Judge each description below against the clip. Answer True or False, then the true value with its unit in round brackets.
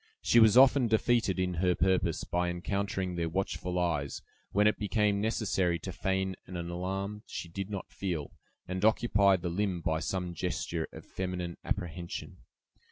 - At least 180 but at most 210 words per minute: False (160 wpm)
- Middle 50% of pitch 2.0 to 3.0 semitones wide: True (2.6 semitones)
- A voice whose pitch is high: False (95 Hz)